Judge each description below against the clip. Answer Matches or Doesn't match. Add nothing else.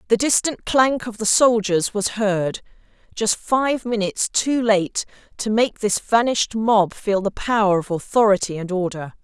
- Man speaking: Doesn't match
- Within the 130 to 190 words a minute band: Matches